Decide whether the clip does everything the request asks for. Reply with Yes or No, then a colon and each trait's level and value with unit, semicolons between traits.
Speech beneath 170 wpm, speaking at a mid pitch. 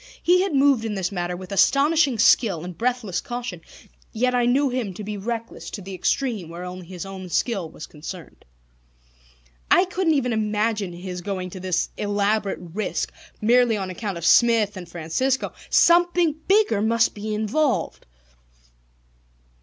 No: average, 155 wpm; high, 215 Hz